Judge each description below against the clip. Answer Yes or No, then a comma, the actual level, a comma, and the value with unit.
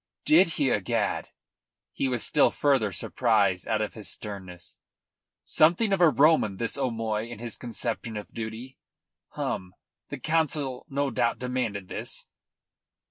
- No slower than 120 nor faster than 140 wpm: Yes, slow, 135 wpm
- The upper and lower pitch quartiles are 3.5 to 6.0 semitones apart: Yes, average, 4.6 semitones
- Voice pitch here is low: Yes, low, 120 Hz